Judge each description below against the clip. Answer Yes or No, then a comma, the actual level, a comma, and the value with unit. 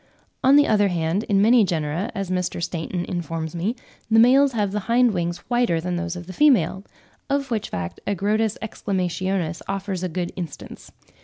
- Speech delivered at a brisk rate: No, average, 170 wpm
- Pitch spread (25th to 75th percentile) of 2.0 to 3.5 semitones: No, average, 4.3 semitones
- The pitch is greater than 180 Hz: Yes, high, 190 Hz